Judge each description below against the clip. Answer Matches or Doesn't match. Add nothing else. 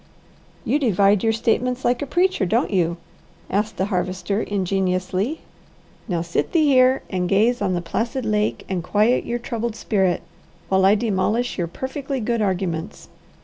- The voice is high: Matches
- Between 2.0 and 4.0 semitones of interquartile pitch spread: Doesn't match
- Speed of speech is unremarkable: Matches